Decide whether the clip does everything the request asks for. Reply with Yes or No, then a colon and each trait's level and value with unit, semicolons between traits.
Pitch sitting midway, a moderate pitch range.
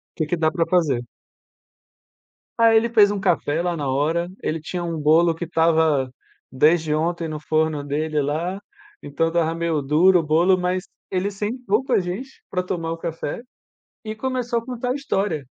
Yes: medium, 170 Hz; average, 3.7 semitones